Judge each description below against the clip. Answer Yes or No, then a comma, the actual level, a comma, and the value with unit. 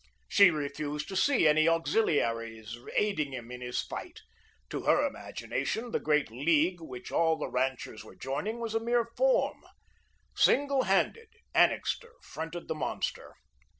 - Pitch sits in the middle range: Yes, medium, 160 Hz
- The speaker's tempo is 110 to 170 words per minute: Yes, average, 145 wpm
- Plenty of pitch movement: Yes, wide, 8.9 semitones